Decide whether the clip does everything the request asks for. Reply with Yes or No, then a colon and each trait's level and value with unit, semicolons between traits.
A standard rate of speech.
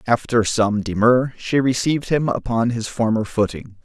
Yes: average, 155 wpm